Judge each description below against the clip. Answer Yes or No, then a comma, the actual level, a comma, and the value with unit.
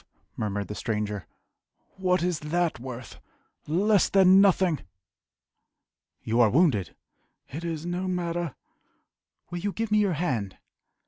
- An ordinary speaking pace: No, slow, 125 wpm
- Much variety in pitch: Yes, wide, 7.6 semitones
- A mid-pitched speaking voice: Yes, medium, 170 Hz